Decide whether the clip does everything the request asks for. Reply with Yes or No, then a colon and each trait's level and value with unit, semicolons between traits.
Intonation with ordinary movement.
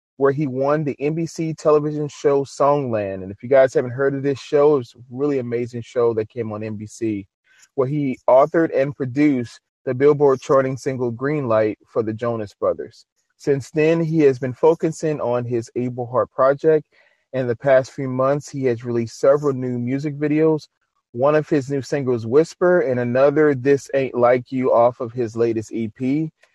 Yes: average, 3.4 semitones